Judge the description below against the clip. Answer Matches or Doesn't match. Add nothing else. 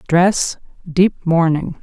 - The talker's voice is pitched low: Doesn't match